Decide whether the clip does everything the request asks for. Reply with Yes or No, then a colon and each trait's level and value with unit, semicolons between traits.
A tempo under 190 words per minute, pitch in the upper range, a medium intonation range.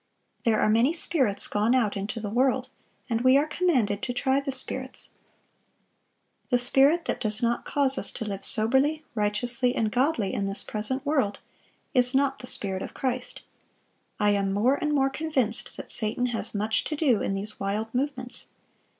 Yes: average, 180 wpm; high, 245 Hz; average, 4.1 semitones